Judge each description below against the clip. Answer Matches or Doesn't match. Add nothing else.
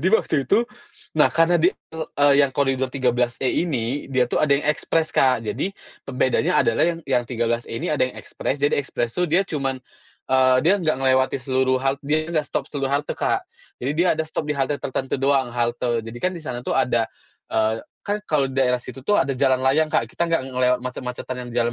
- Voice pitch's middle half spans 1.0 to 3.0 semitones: Doesn't match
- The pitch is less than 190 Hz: Matches